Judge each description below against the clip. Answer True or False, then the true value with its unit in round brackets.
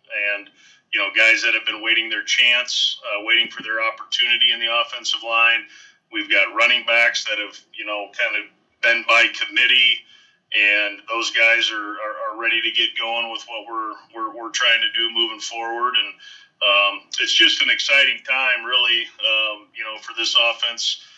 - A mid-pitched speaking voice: False (115 Hz)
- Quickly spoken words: False (185 wpm)